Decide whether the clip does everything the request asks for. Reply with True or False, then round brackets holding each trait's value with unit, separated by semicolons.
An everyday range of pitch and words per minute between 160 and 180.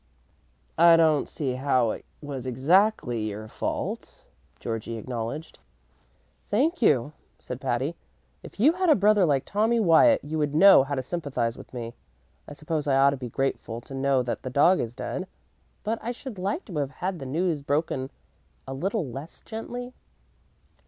False (6.8 semitones; 170 wpm)